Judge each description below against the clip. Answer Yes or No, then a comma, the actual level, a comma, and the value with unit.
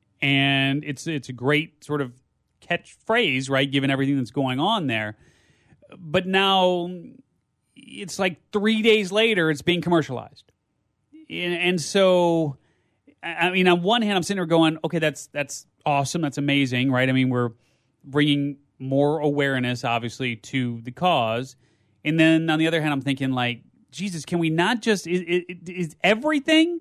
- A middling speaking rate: Yes, average, 155 wpm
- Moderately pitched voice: Yes, medium, 155 Hz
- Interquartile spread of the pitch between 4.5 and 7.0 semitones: Yes, average, 4.8 semitones